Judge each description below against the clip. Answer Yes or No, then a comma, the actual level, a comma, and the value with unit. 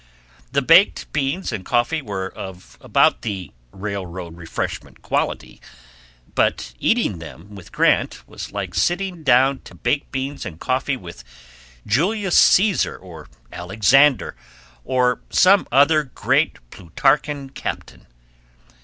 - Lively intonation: Yes, wide, 7.8 semitones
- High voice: No, low, 130 Hz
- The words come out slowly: Yes, slow, 120 wpm